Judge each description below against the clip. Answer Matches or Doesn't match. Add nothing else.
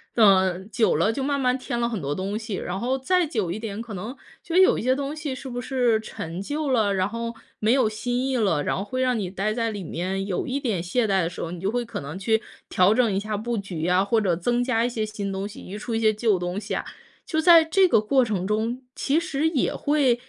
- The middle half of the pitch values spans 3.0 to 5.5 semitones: Matches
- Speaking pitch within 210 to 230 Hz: Matches